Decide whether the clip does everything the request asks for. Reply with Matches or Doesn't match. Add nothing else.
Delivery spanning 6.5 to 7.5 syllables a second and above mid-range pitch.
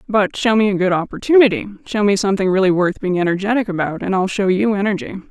Matches